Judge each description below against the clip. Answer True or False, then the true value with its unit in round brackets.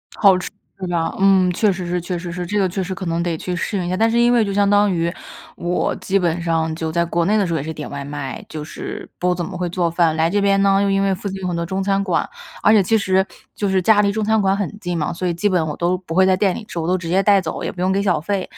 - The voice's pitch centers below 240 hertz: True (185 Hz)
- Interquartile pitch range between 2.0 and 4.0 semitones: True (2.5 semitones)